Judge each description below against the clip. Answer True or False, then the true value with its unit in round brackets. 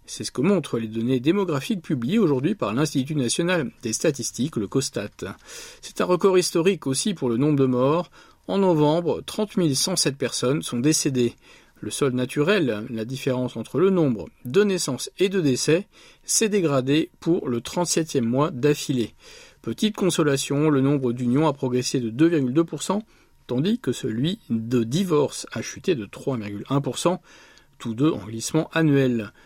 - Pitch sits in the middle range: True (145 Hz)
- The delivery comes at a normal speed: True (155 wpm)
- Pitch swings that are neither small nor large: False (5.8 semitones)